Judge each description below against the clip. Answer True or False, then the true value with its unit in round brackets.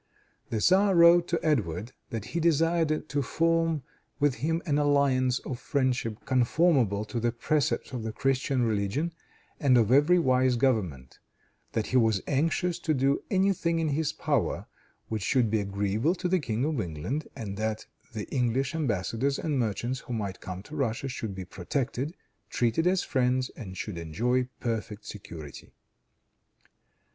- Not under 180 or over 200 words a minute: False (160 wpm)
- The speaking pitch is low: True (130 Hz)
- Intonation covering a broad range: True (5.8 semitones)